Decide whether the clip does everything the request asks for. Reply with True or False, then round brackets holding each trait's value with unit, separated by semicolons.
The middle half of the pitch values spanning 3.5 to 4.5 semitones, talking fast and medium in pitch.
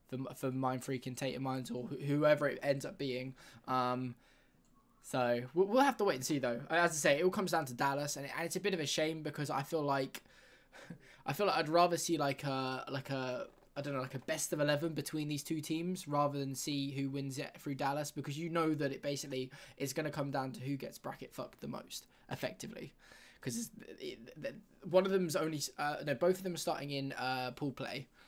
True (3.9 semitones; 225 wpm; 145 Hz)